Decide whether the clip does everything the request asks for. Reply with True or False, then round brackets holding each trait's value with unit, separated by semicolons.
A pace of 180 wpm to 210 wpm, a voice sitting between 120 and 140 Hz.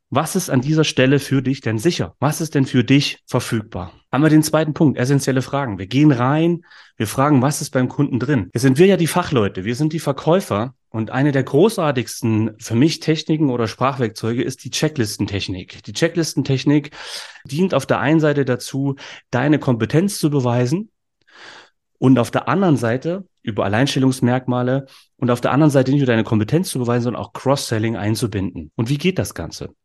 True (185 wpm; 135 Hz)